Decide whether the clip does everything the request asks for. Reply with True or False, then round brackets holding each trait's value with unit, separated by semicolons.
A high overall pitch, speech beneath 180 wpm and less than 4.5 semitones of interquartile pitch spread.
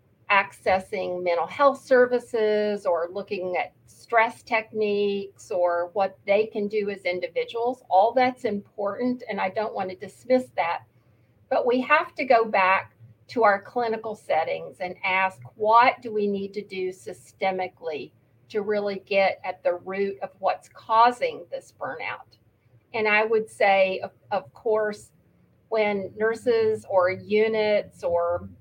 True (205 Hz; 145 wpm; 3.4 semitones)